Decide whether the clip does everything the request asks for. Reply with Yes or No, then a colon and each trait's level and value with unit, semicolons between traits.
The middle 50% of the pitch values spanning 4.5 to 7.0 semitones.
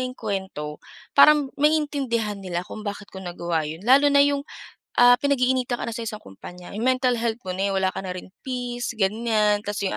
Yes: average, 5.0 semitones